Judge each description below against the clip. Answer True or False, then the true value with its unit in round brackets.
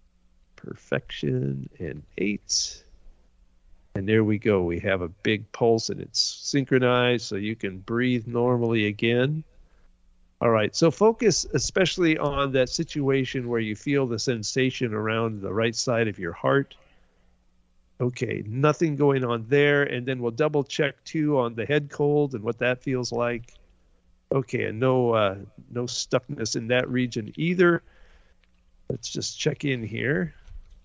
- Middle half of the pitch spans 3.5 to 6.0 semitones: True (5.6 semitones)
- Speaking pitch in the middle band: False (120 Hz)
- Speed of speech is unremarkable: True (150 wpm)